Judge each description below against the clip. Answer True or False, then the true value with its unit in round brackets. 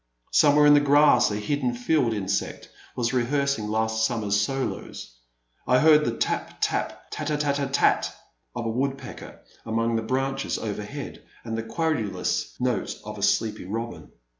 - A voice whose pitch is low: True (120 Hz)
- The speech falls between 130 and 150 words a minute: False (160 wpm)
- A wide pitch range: False (4.0 semitones)